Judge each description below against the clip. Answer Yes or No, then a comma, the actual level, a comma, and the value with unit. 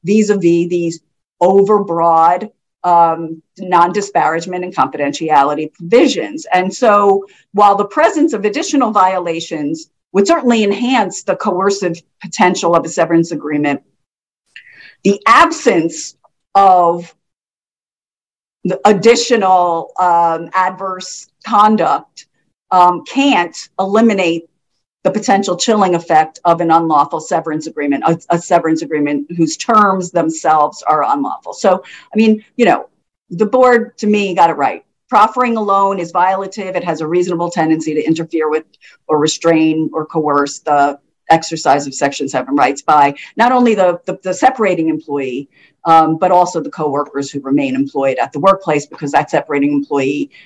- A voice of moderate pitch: Yes, medium, 175 Hz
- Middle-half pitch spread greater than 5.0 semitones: No, average, 4.2 semitones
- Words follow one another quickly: No, slow, 135 wpm